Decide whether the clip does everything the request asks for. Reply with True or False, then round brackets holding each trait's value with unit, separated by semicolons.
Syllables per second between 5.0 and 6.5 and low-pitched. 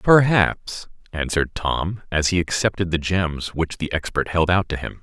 False (4.6 syllables/s; 90 Hz)